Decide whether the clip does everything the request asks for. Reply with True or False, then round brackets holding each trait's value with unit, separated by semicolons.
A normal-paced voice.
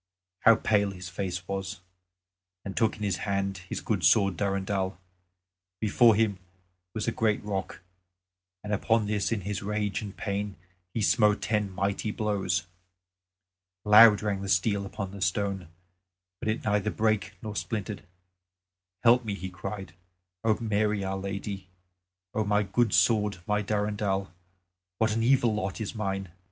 True (150 wpm)